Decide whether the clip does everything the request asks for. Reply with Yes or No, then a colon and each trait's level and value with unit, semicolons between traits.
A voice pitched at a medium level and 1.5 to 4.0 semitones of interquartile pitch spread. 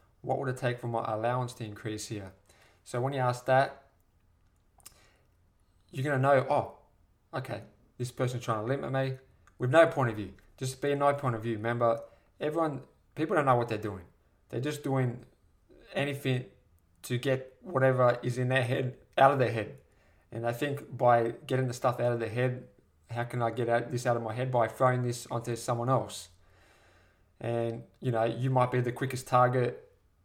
No: low, 120 Hz; average, 3.5 semitones